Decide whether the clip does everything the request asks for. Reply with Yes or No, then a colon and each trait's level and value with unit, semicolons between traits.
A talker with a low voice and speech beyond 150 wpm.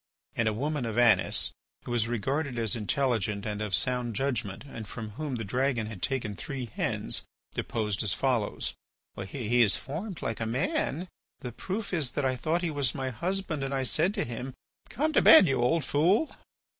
Yes: low, 125 Hz; average, 190 wpm